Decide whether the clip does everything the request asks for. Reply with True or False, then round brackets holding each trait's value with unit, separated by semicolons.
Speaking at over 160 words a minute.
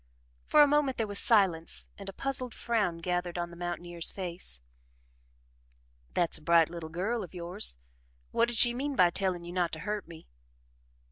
True (180 wpm)